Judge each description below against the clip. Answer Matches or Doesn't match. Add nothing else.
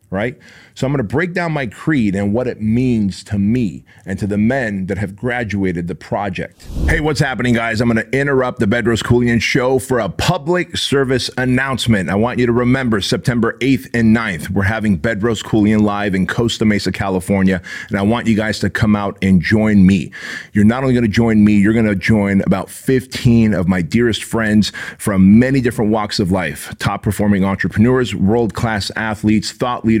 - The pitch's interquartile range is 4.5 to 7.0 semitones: Doesn't match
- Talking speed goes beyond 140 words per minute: Matches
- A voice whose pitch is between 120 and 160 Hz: Doesn't match